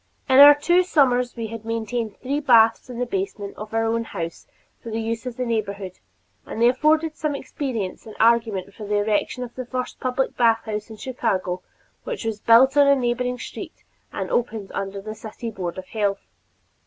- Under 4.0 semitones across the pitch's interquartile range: Yes, average, 3.1 semitones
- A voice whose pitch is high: Yes, high, 230 Hz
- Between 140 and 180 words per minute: No, average, 195 wpm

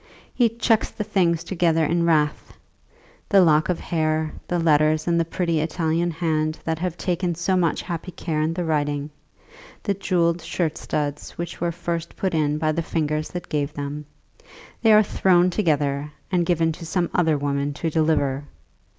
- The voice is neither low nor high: Yes, medium, 165 Hz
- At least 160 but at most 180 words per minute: Yes, average, 175 wpm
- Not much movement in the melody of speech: Yes, narrow, 2.3 semitones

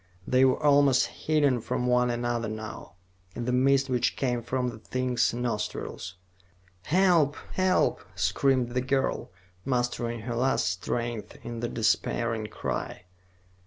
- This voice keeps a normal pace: No, slow, 130 wpm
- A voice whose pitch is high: No, low, 125 Hz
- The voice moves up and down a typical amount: No, narrow, 2.2 semitones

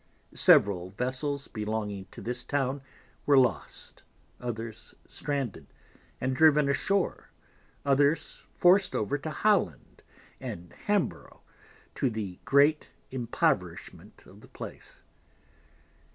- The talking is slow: Yes, slow, 100 wpm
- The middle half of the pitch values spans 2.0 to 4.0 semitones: No, average, 4.9 semitones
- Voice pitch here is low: Yes, low, 130 Hz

